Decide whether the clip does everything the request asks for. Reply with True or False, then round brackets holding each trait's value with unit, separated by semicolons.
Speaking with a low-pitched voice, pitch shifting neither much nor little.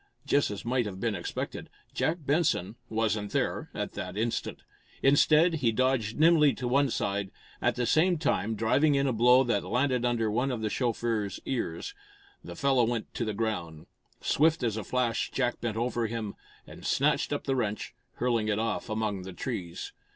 True (120 Hz; 3.6 semitones)